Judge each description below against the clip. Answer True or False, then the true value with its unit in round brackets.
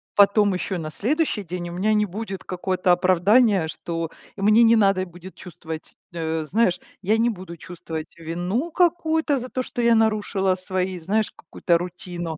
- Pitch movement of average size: True (4.0 semitones)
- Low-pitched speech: False (190 Hz)